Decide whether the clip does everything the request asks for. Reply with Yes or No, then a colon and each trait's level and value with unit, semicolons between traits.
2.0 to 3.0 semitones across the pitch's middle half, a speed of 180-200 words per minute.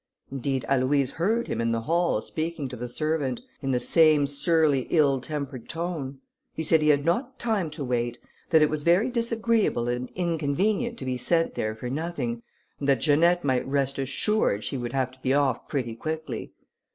No: average, 4.5 semitones; average, 190 wpm